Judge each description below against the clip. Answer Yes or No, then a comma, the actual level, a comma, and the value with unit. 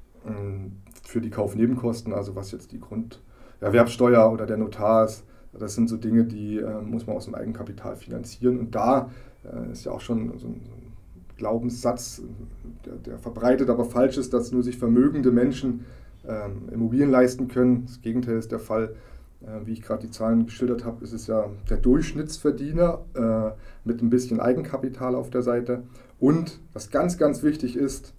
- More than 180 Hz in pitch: No, low, 120 Hz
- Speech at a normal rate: Yes, average, 170 wpm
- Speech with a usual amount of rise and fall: No, narrow, 2.1 semitones